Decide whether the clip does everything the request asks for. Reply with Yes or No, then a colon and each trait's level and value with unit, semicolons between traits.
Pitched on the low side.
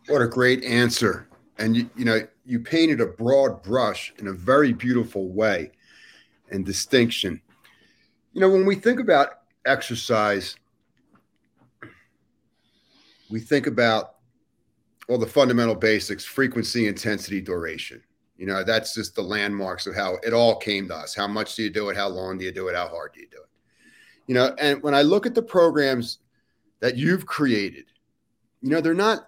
Yes: low, 115 Hz